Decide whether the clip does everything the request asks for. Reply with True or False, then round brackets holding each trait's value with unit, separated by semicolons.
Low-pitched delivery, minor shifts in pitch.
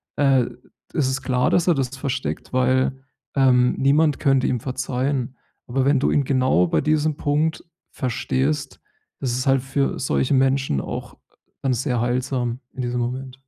True (130 Hz; 1.6 semitones)